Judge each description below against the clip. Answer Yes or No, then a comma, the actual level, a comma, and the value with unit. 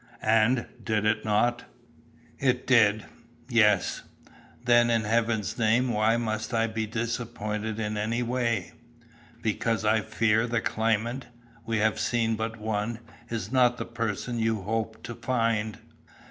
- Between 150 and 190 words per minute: No, slow, 135 wpm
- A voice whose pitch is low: Yes, low, 115 Hz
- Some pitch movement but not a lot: No, narrow, 1.5 semitones